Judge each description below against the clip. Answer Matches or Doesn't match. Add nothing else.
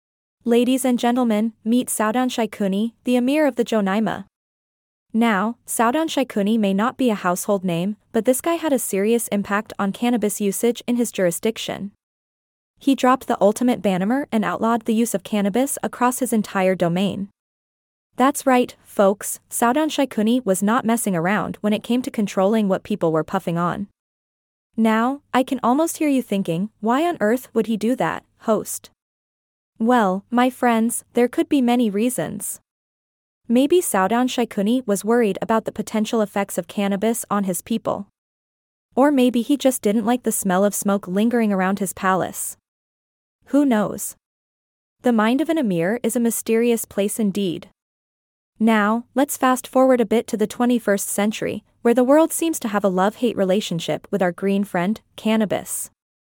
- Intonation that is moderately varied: Matches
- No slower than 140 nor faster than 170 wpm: Matches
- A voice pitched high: Matches